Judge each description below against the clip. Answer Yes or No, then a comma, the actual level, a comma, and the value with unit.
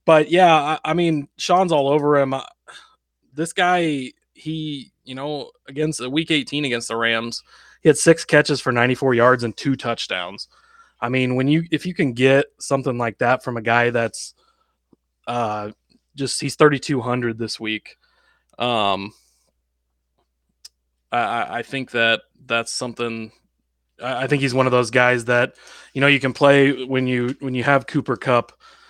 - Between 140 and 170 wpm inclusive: Yes, average, 165 wpm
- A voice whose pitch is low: Yes, low, 130 Hz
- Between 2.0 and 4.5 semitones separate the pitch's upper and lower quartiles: Yes, average, 3.7 semitones